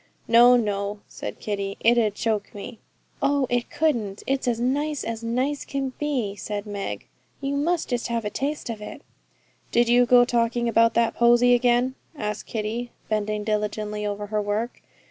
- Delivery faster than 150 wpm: Yes, average, 170 wpm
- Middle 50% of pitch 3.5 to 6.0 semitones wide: No, average, 2.8 semitones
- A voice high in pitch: Yes, high, 235 Hz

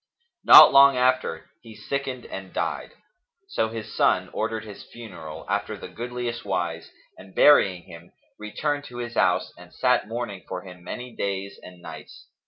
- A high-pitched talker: No, low, 110 Hz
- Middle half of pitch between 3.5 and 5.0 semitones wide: Yes, average, 4.7 semitones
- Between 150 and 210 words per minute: Yes, average, 160 wpm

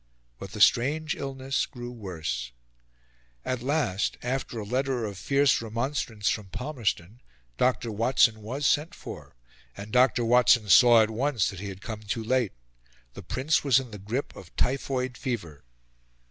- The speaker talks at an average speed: Yes, average, 155 wpm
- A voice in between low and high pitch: No, low, 120 Hz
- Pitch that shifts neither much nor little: Yes, average, 3.9 semitones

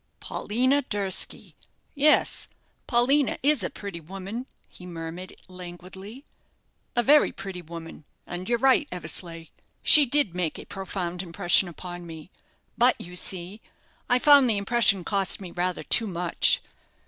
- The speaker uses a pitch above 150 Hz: Yes, high, 190 Hz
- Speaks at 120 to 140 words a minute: Yes, slow, 135 wpm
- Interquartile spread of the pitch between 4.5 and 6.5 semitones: Yes, average, 5.3 semitones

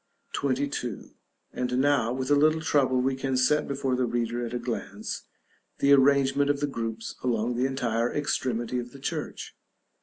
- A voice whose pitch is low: Yes, low, 130 Hz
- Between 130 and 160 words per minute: No, average, 175 wpm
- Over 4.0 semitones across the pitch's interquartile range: No, narrow, 2.6 semitones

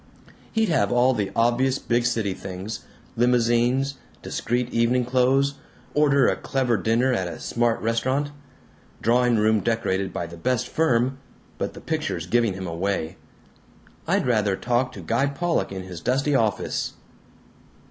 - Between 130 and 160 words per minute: Yes, average, 145 wpm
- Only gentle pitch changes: No, average, 3.6 semitones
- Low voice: Yes, low, 120 Hz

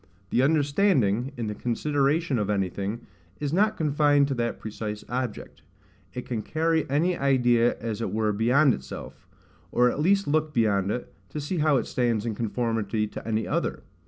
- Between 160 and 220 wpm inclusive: Yes, average, 170 wpm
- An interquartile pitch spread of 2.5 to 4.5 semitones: No, average, 5.0 semitones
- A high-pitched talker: No, low, 125 Hz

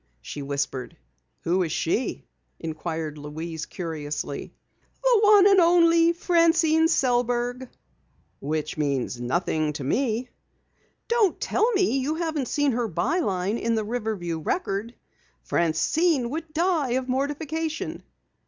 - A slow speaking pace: Yes, slow, 120 wpm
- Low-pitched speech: No, high, 245 Hz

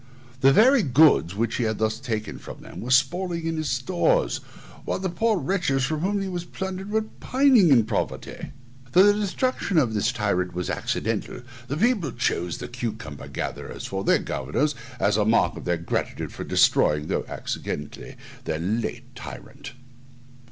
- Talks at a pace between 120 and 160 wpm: No, average, 170 wpm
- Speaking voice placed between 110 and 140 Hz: Yes, low, 135 Hz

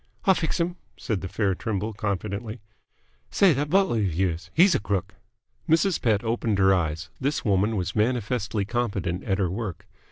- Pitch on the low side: Yes, low, 105 Hz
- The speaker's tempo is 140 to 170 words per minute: Yes, average, 165 wpm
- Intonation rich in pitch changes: No, average, 4.1 semitones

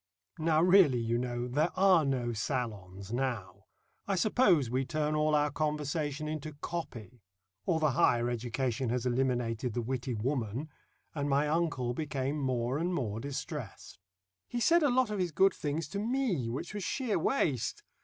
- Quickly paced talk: No, average, 165 wpm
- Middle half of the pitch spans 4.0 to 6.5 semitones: Yes, average, 5.0 semitones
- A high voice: No, medium, 140 Hz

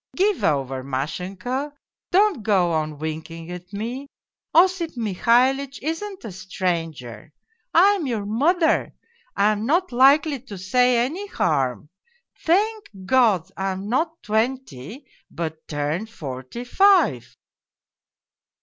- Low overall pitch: No, high, 225 Hz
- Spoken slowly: Yes, slow, 115 wpm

